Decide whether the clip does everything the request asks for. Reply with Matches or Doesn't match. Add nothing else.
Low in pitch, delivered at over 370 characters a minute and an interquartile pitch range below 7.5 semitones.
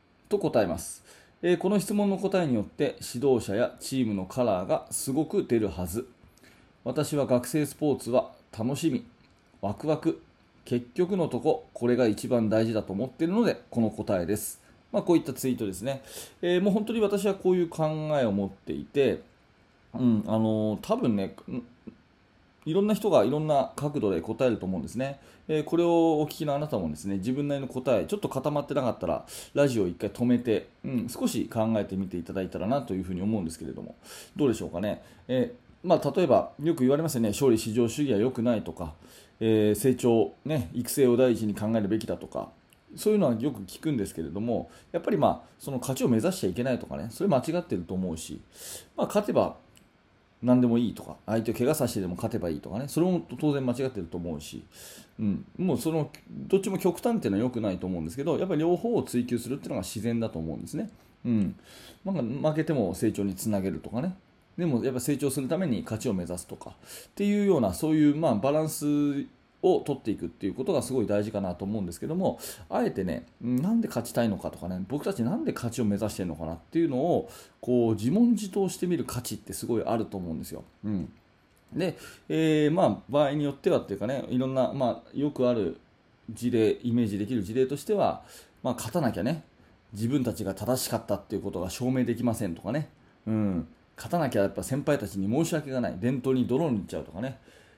Matches